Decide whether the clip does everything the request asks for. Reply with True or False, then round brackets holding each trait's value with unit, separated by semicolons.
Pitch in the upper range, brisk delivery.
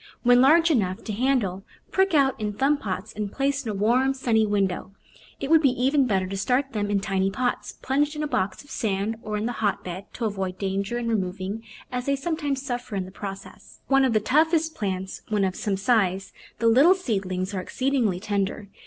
True (220 Hz; 210 wpm)